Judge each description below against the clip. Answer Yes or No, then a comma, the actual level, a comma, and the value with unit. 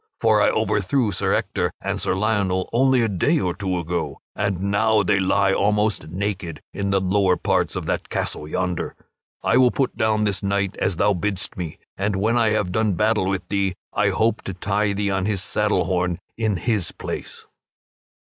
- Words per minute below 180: No, average, 190 wpm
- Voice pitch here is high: No, low, 100 Hz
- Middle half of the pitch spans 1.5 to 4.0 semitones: Yes, narrow, 2.4 semitones